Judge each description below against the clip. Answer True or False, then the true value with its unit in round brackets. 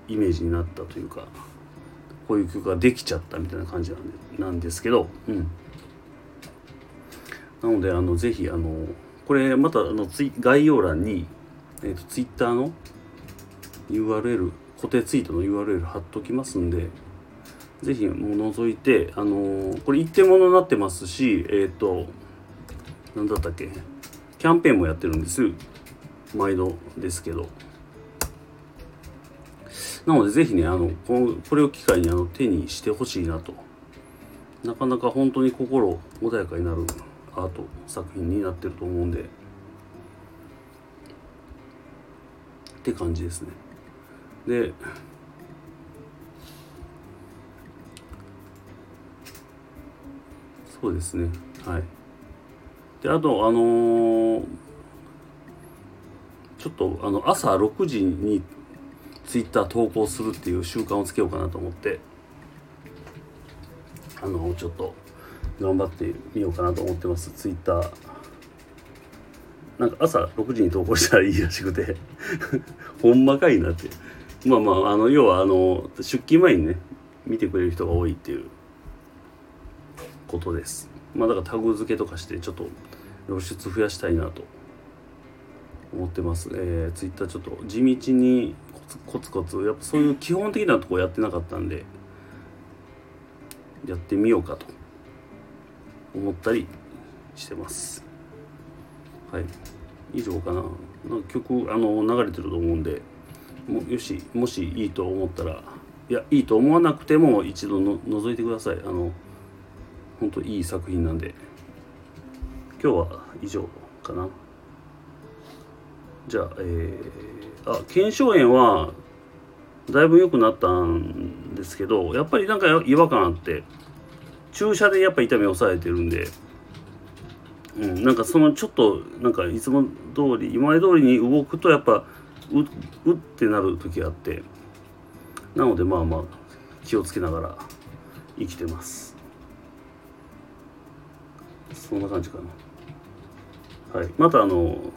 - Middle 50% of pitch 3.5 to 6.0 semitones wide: False (6.8 semitones)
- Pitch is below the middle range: True (95 Hz)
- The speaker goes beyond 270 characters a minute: False (255 characters per minute)